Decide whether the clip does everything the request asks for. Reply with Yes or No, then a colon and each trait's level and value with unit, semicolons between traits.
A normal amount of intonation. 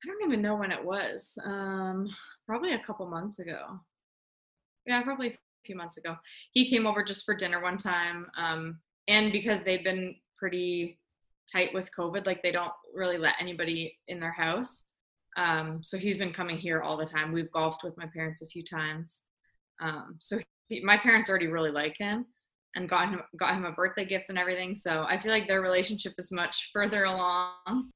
Yes: average, 3.3 semitones